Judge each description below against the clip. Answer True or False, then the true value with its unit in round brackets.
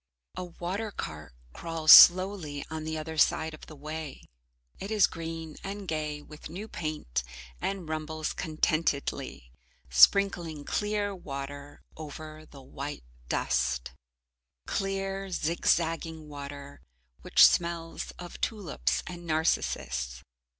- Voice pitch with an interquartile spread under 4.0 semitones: True (3.3 semitones)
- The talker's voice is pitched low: False (160 Hz)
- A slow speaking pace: True (115 wpm)